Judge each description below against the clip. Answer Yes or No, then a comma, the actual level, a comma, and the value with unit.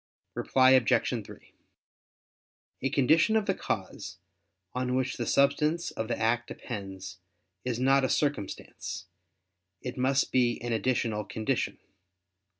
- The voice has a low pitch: Yes, low, 125 Hz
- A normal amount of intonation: Yes, average, 3.4 semitones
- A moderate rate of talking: No, slow, 125 wpm